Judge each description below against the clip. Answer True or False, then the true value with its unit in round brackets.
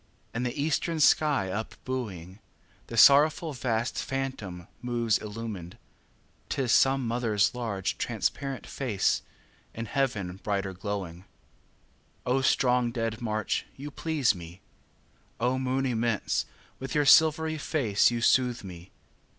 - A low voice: True (120 Hz)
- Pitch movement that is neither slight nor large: True (4.7 semitones)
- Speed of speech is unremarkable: False (125 wpm)